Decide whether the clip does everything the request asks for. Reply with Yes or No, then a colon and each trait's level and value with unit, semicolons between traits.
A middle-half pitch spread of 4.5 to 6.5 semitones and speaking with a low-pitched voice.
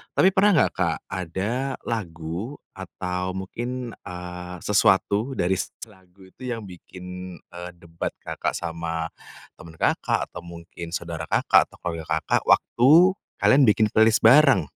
Yes: average, 4.8 semitones; very low, 95 Hz